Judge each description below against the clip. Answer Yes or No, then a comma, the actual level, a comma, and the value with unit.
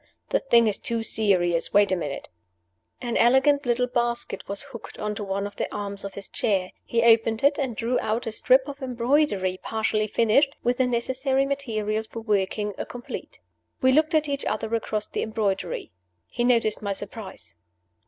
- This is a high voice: Yes, high, 225 Hz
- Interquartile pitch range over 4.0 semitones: No, average, 3.7 semitones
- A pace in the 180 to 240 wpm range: Yes, average, 185 wpm